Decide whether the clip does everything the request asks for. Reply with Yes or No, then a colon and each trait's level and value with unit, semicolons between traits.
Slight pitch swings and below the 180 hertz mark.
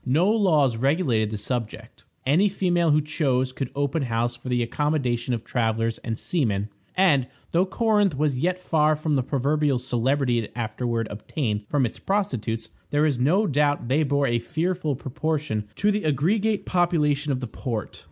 No: average, 4.9 semitones; medium, 140 Hz